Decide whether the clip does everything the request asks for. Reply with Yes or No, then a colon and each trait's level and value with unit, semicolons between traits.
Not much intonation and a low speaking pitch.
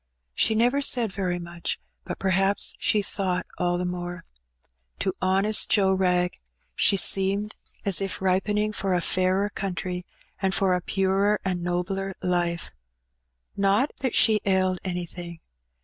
No: narrow, 1.9 semitones; high, 190 Hz